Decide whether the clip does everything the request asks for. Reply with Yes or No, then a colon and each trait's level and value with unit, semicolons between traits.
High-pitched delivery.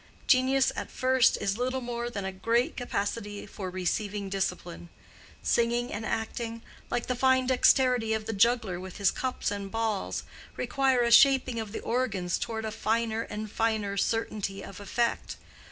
Yes: high, 225 Hz